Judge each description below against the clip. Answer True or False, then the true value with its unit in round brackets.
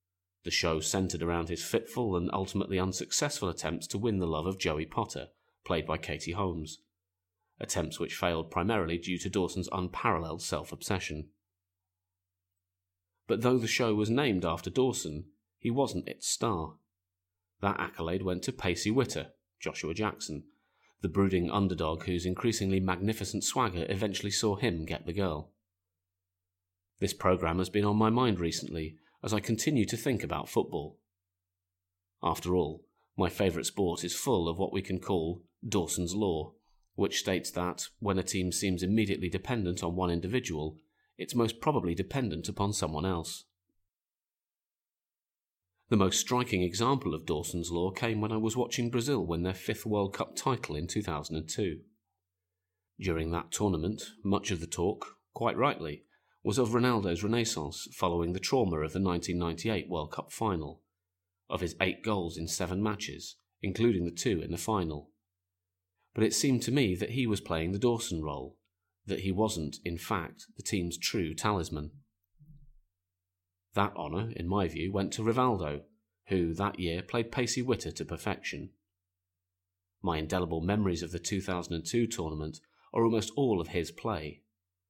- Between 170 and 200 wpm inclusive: False (155 wpm)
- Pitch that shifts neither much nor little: True (3.4 semitones)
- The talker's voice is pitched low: True (90 Hz)